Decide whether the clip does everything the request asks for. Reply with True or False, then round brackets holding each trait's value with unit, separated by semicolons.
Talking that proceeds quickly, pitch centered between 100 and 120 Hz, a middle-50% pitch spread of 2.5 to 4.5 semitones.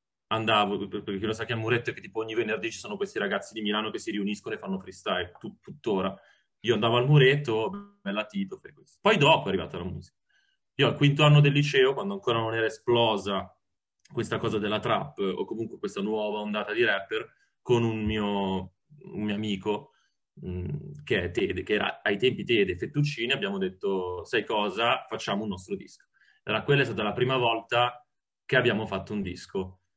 False (195 wpm; 110 Hz; 5.6 semitones)